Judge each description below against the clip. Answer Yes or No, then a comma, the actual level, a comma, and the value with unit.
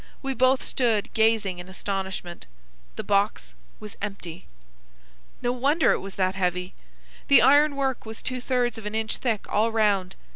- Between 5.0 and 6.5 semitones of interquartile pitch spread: No, average, 4.6 semitones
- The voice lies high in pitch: Yes, high, 215 Hz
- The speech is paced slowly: No, average, 160 wpm